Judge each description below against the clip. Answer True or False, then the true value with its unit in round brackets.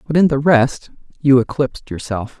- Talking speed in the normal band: True (175 wpm)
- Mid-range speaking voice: False (130 Hz)